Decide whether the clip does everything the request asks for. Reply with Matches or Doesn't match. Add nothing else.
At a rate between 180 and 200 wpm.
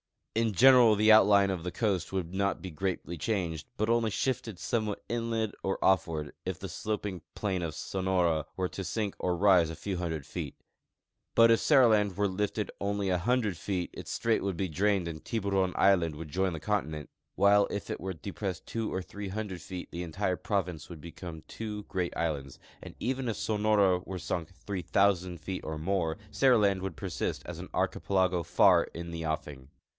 Matches